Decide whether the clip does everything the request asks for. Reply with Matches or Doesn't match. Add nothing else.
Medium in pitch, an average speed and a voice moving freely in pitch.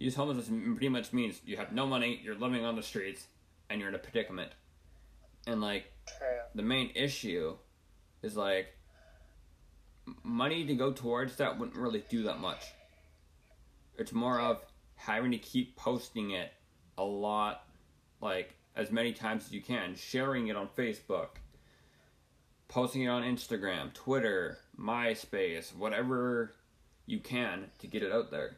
Doesn't match